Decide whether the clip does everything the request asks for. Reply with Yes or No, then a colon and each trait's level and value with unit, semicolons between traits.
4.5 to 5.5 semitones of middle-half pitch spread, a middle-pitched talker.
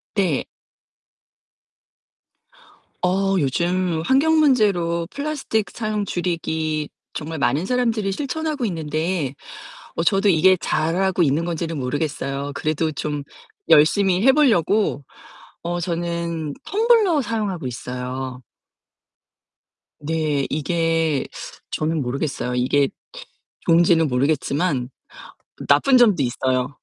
Yes: average, 5.1 semitones; medium, 170 Hz